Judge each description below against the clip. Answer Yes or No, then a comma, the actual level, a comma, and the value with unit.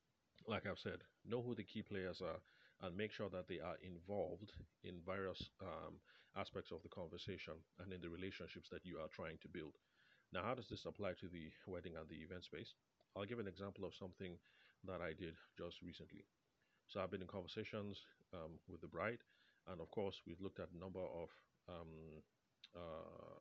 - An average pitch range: No, narrow, 2.3 semitones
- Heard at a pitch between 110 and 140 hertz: No, very low, 95 Hz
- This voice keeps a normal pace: Yes, average, 195 wpm